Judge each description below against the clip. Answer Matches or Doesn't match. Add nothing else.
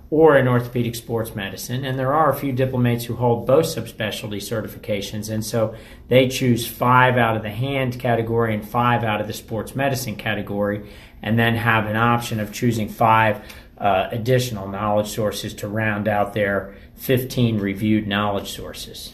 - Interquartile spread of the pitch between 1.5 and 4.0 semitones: Matches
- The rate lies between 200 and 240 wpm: Doesn't match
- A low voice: Matches